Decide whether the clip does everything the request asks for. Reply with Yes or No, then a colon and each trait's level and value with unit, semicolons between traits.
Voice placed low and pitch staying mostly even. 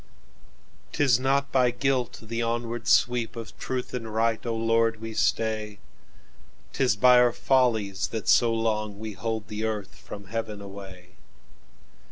Yes: low, 115 Hz; narrow, 2.3 semitones